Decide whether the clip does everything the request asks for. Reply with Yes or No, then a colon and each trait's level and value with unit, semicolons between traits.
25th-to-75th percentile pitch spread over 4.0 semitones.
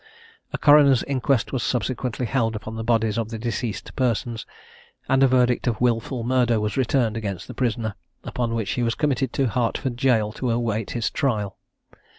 No: narrow, 2.5 semitones